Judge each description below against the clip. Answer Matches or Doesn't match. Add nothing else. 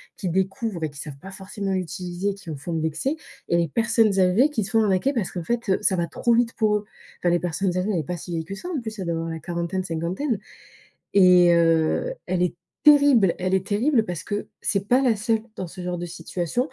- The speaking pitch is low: Doesn't match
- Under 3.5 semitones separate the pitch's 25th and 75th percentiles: Doesn't match